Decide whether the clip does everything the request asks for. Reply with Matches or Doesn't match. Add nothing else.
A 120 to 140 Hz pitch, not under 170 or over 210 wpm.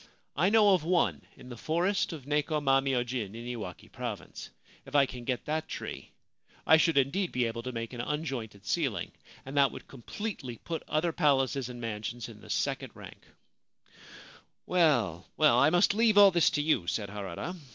Matches